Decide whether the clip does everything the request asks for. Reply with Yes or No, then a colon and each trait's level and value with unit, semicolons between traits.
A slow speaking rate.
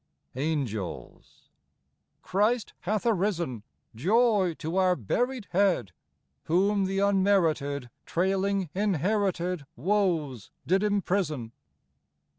Yes: slow, 80 wpm